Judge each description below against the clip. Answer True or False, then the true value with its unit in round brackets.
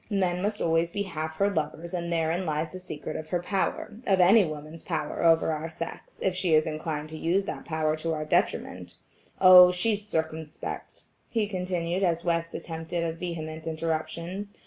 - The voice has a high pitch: False (170 Hz)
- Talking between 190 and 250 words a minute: False (175 wpm)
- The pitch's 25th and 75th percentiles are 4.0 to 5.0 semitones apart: False (2.6 semitones)